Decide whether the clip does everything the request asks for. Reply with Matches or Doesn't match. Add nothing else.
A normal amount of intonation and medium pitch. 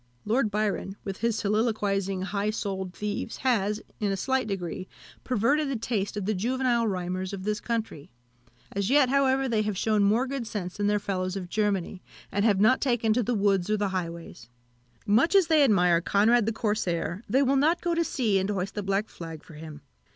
Doesn't match